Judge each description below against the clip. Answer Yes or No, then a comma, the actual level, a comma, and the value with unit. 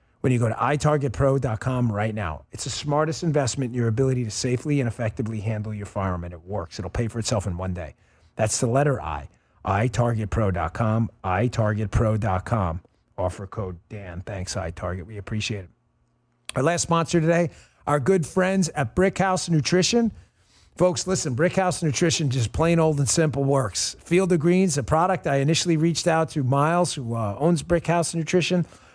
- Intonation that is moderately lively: No, wide, 7.0 semitones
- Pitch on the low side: Yes, low, 130 Hz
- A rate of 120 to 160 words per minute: No, average, 170 wpm